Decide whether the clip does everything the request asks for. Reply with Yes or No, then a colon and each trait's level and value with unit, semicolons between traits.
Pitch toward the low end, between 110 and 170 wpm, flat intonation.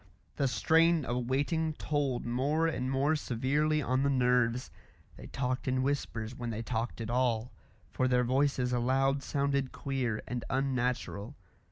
Yes: low, 130 Hz; average, 150 wpm; narrow, 2.3 semitones